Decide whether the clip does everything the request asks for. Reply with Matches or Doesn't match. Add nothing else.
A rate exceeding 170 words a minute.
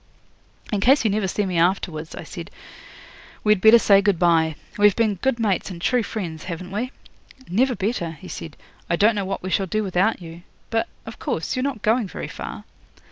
Matches